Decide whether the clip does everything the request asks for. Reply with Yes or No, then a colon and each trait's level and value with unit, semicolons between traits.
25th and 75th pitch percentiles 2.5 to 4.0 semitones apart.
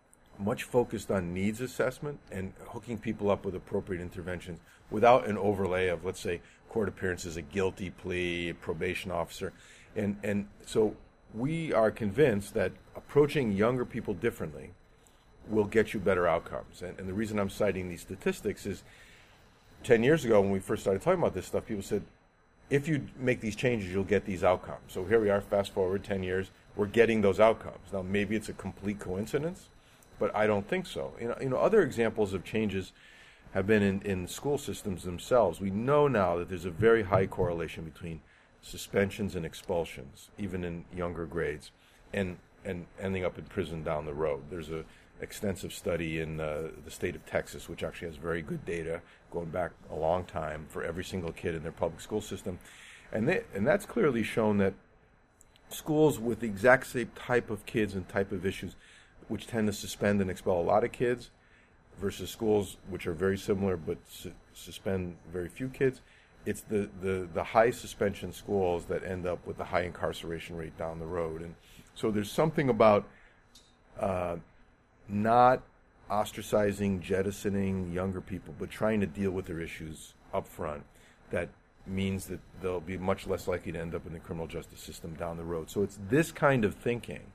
Yes: average, 3.5 semitones